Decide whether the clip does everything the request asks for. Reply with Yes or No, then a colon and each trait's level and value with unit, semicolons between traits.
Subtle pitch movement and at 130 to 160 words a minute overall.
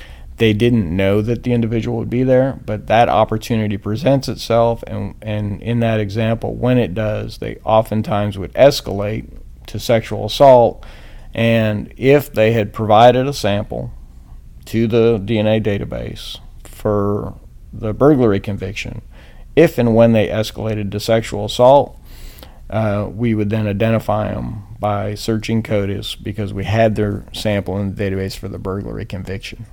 Yes: narrow, 2.1 semitones; average, 145 wpm